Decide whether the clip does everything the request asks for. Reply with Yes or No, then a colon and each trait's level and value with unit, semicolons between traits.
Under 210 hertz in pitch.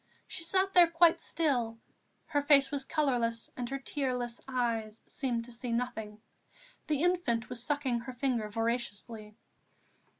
No: very high, 250 Hz